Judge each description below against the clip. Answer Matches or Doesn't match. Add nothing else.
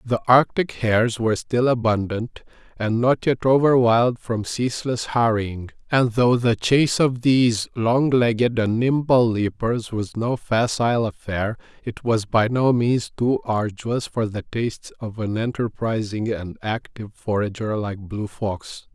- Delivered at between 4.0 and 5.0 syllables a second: Matches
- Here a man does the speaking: Matches